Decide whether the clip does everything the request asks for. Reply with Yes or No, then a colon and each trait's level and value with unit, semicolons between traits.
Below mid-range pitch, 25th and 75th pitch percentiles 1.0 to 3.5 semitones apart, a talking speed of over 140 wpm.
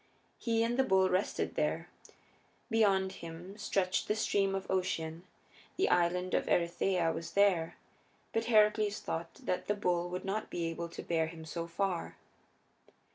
No: medium, 185 Hz; average, 3.2 semitones; average, 155 wpm